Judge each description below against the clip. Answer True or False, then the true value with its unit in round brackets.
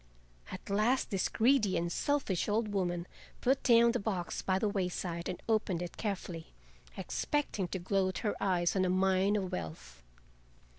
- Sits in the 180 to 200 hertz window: True (190 Hz)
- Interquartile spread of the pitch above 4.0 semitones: False (3.4 semitones)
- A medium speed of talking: True (160 wpm)